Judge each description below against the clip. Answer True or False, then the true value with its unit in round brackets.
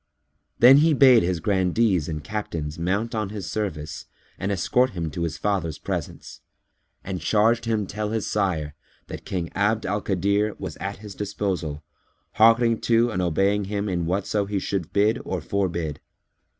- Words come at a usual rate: True (165 wpm)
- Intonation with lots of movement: False (3.7 semitones)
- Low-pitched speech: True (100 Hz)